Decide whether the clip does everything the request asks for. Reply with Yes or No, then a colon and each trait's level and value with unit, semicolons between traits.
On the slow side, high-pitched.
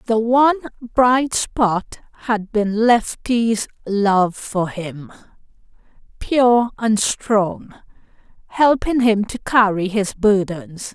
Yes: slow, 105 wpm; high, 220 Hz